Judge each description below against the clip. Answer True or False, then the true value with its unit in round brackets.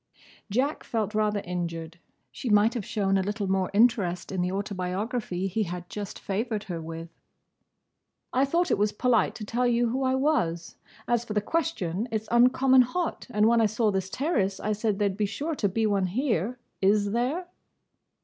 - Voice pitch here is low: False (210 Hz)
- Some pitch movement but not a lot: True (4.1 semitones)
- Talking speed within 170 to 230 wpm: True (190 wpm)